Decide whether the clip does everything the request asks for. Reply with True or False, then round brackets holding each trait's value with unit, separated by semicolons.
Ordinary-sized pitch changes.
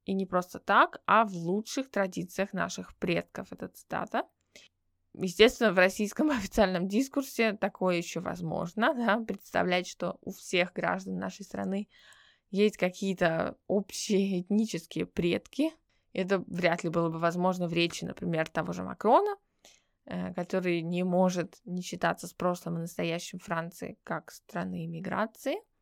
True (3.5 semitones)